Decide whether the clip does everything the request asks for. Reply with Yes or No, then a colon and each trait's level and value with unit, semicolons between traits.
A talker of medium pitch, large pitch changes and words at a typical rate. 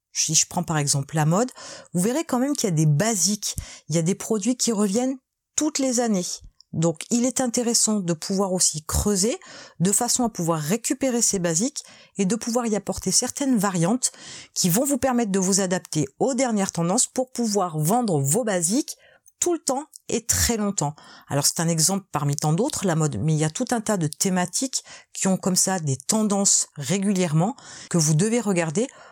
No: high, 200 Hz; wide, 6.3 semitones; average, 200 wpm